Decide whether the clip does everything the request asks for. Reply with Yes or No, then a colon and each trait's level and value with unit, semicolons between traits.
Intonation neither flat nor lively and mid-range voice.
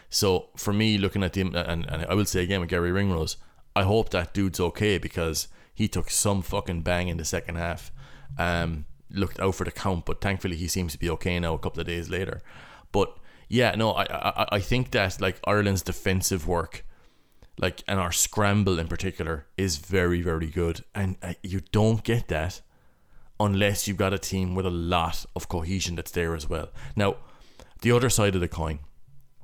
No: average, 3.0 semitones; very low, 95 Hz